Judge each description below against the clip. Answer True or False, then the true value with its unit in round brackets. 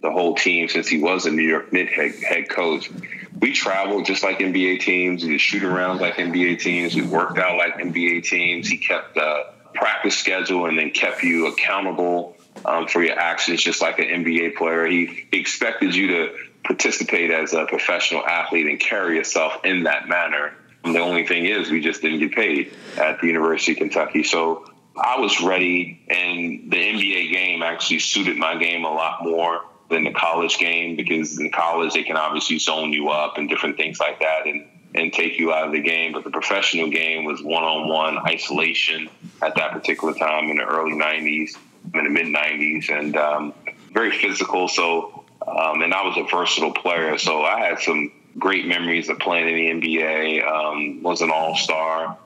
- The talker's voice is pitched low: True (80 Hz)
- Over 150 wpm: True (195 wpm)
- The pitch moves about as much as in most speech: False (1.7 semitones)